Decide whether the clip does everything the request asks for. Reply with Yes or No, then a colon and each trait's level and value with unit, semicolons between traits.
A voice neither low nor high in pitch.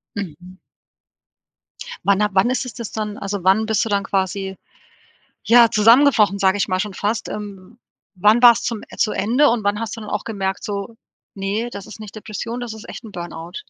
No: high, 210 Hz